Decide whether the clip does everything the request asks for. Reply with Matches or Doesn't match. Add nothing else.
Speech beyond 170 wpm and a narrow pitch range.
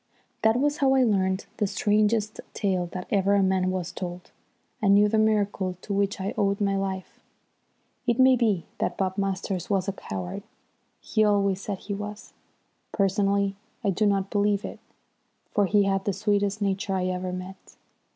Matches